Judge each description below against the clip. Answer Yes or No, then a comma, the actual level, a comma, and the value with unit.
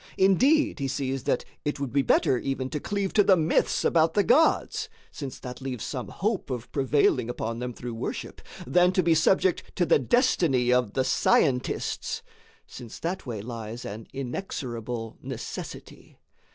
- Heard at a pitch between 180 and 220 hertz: No, low, 135 Hz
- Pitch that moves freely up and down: Yes, wide, 6.2 semitones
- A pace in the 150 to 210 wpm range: Yes, average, 165 wpm